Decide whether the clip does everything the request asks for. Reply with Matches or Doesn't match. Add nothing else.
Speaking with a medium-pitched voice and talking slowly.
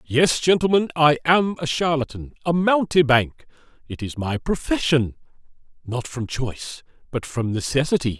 Matches